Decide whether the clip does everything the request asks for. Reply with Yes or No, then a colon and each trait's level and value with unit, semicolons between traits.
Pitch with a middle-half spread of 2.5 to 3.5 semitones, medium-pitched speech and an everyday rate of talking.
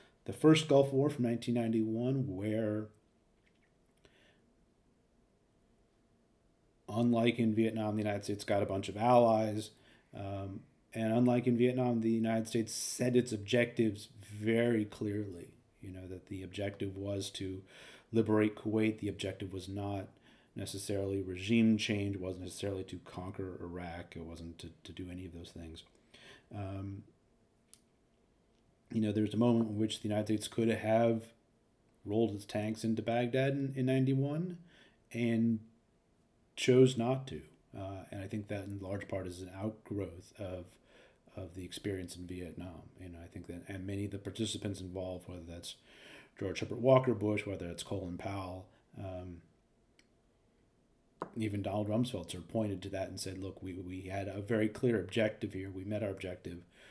No: average, 3.2 semitones; low, 105 Hz; average, 160 wpm